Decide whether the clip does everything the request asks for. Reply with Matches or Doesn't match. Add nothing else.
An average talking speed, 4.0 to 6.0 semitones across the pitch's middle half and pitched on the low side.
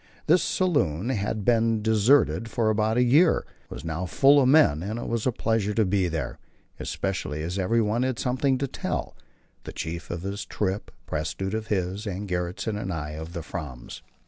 Matches